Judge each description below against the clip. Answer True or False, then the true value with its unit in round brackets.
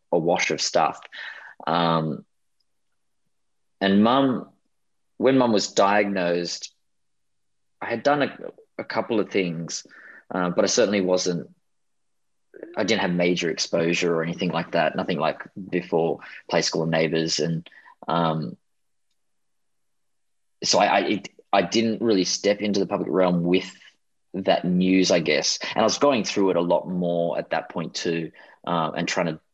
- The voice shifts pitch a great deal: False (3.1 semitones)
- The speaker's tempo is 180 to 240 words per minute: False (155 wpm)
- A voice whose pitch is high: False (90 Hz)